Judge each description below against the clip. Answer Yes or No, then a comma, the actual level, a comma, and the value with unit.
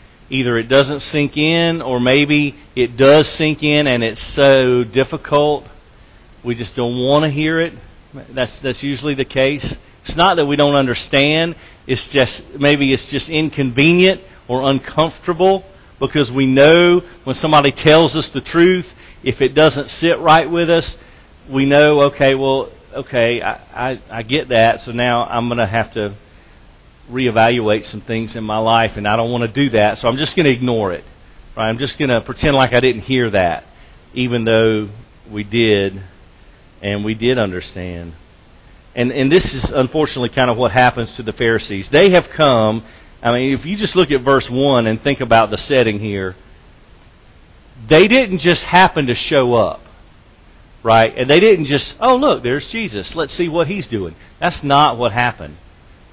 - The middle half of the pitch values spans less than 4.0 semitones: No, average, 4.6 semitones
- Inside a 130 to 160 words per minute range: No, average, 175 wpm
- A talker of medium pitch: No, low, 125 Hz